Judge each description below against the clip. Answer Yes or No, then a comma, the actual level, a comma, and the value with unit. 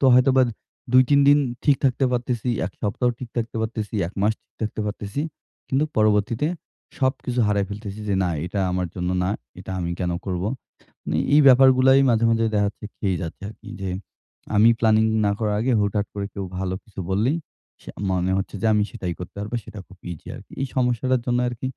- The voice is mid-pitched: No, low, 110 Hz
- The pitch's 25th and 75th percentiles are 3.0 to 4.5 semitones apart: Yes, average, 4.0 semitones